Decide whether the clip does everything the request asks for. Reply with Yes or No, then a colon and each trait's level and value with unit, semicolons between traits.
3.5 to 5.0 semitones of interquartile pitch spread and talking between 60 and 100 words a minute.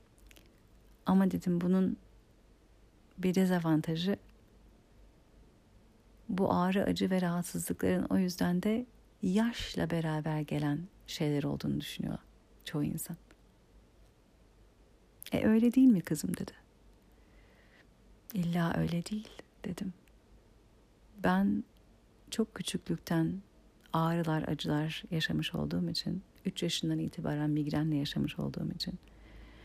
Yes: average, 4.1 semitones; slow, 95 wpm